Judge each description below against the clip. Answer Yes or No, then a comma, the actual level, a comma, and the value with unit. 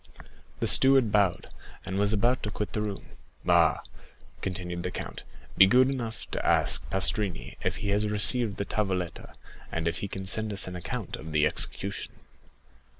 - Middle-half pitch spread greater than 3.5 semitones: No, average, 2.8 semitones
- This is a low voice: Yes, low, 100 Hz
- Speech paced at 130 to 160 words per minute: No, average, 170 wpm